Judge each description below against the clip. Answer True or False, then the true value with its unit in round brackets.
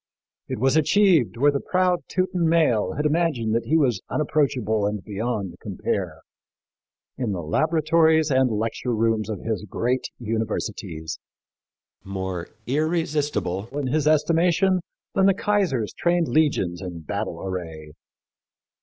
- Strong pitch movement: True (7.5 semitones)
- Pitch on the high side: False (125 Hz)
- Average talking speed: False (130 wpm)